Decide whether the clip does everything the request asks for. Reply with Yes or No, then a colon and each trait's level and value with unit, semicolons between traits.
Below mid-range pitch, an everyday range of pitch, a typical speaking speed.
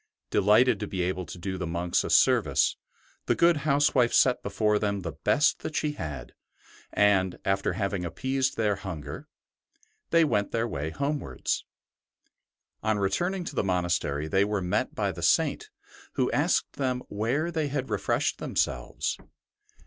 No: low, 105 Hz; wide, 6.7 semitones; average, 155 wpm